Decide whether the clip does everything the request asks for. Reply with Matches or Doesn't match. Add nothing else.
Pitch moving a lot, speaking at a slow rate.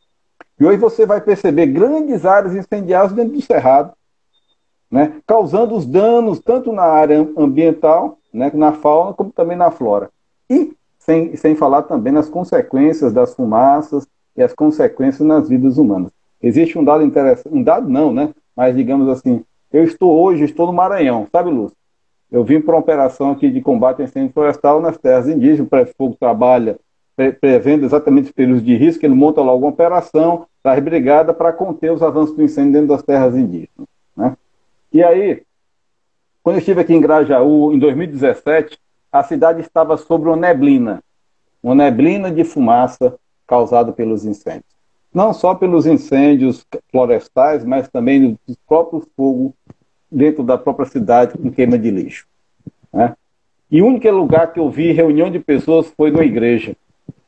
Doesn't match